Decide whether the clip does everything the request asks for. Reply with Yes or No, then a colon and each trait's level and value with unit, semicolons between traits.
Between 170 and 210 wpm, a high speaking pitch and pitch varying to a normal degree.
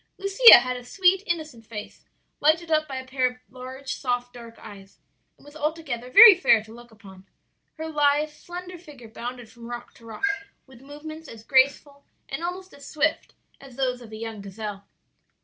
Yes: average, 185 wpm; very high, 260 Hz; average, 5.0 semitones